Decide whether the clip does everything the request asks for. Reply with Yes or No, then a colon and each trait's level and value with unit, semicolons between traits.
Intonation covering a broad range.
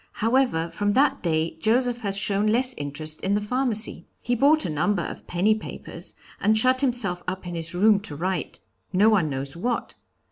Yes: wide, 5.8 semitones